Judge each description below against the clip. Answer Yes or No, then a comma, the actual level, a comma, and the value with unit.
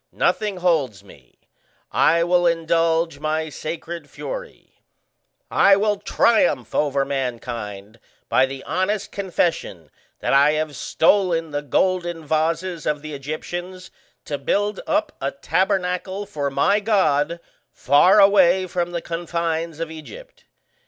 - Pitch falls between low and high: Yes, medium, 165 Hz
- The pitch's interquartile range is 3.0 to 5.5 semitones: Yes, average, 4.3 semitones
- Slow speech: Yes, slow, 125 wpm